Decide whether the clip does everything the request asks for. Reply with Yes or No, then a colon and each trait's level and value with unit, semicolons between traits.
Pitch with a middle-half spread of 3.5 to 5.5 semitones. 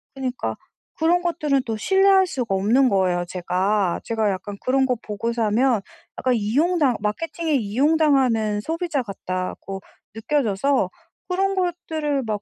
No: wide, 7.1 semitones